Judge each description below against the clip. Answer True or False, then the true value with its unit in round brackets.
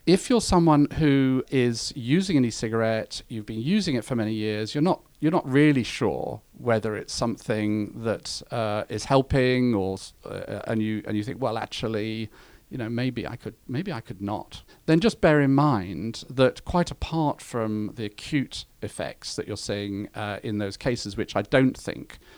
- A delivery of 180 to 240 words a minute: True (190 wpm)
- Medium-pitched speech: False (120 Hz)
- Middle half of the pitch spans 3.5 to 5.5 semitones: True (5.0 semitones)